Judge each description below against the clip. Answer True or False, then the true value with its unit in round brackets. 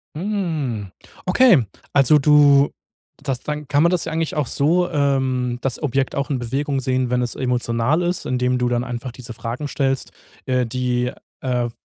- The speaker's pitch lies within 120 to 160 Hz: True (135 Hz)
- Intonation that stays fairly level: False (3.1 semitones)